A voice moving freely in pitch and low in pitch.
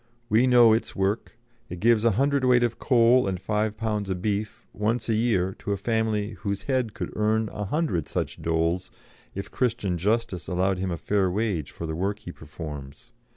No: average, 3.8 semitones; low, 105 Hz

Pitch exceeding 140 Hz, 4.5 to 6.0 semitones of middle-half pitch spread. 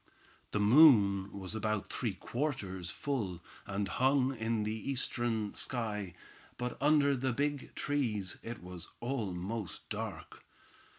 No: low, 110 Hz; average, 4.9 semitones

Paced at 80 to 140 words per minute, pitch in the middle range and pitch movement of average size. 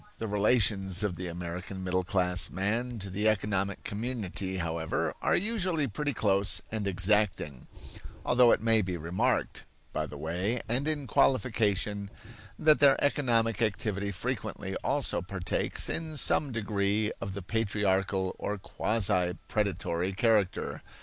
No: slow, 135 wpm; low, 100 Hz; average, 3.5 semitones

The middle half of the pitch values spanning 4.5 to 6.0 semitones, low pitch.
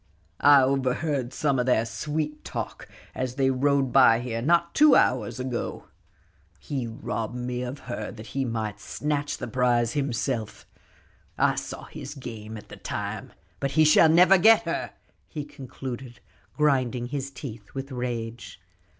No: average, 3.1 semitones; low, 130 Hz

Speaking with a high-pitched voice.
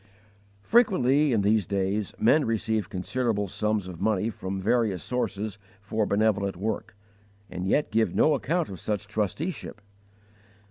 No: low, 110 Hz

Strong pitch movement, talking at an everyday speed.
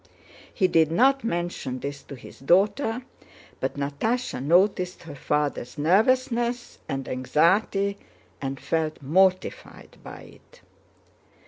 No: wide, 7.0 semitones; slow, 110 wpm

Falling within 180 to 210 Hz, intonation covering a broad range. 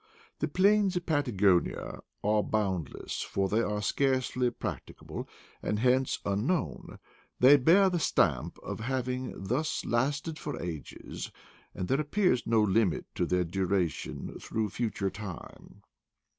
No: low, 115 Hz; wide, 6.3 semitones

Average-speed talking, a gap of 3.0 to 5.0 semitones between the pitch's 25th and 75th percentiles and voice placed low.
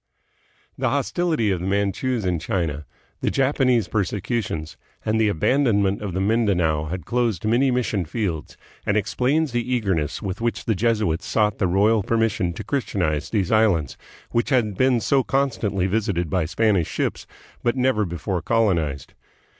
Yes: average, 155 wpm; average, 4.6 semitones; low, 105 Hz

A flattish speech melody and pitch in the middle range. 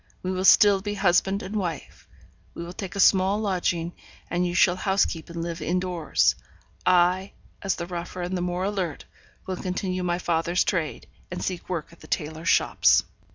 Yes: narrow, 1.7 semitones; medium, 180 Hz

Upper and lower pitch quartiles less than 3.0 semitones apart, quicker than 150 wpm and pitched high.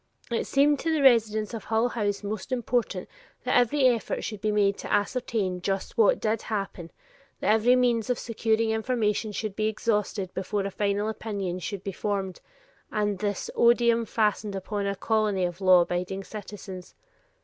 Yes: narrow, 2.6 semitones; average, 170 wpm; high, 210 Hz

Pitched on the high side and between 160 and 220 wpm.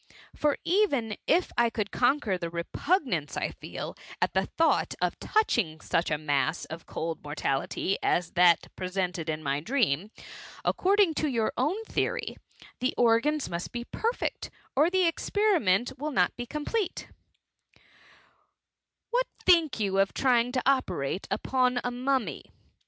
No: high, 240 Hz; average, 150 wpm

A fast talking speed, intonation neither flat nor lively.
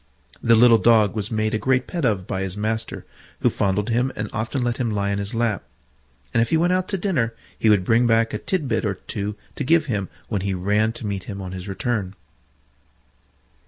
Yes: fast, 225 wpm; average, 3.1 semitones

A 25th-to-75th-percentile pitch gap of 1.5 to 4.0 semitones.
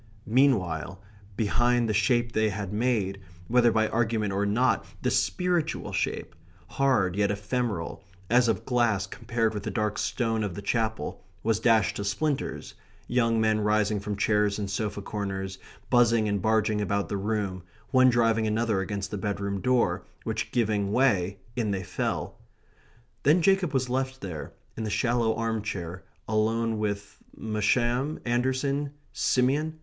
Yes: average, 3.1 semitones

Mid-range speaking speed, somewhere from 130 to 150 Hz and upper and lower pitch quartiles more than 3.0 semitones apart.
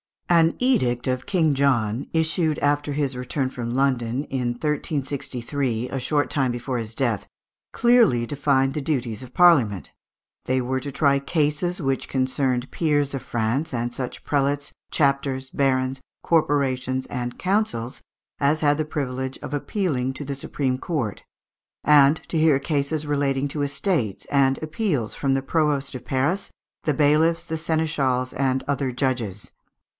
No: average, 150 wpm; medium, 140 Hz; average, 2.7 semitones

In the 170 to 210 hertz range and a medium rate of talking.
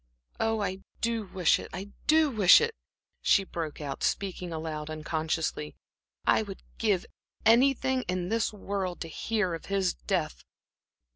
Yes: high, 190 Hz; average, 145 wpm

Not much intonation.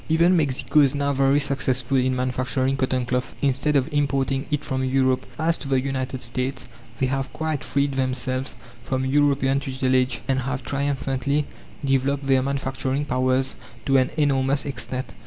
Yes: narrow, 1.4 semitones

